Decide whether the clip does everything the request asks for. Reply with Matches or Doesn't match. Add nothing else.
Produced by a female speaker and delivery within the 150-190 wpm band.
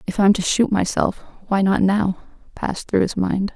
Doesn't match